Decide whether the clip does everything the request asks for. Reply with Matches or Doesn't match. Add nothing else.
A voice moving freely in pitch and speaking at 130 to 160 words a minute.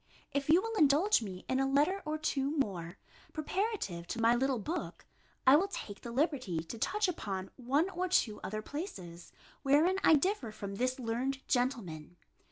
Doesn't match